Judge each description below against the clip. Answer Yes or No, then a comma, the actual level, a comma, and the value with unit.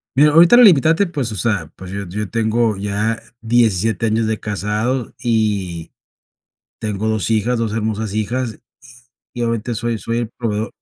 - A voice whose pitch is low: Yes, low, 110 Hz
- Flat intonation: Yes, narrow, 2.2 semitones